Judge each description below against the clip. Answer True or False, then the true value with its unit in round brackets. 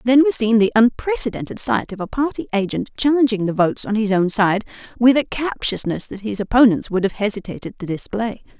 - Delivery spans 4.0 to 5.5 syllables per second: False (5.8 syllables/s)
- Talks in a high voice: True (220 Hz)